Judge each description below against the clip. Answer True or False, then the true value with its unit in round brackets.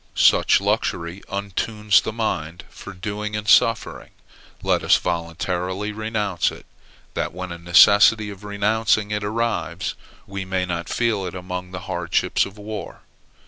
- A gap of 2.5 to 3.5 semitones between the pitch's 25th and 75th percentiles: True (2.8 semitones)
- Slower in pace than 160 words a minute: True (145 wpm)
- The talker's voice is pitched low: True (100 Hz)